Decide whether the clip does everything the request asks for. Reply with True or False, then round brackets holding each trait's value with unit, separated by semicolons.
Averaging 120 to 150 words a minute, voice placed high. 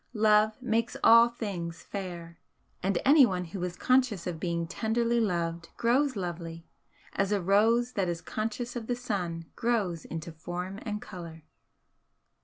True (145 wpm; 195 Hz)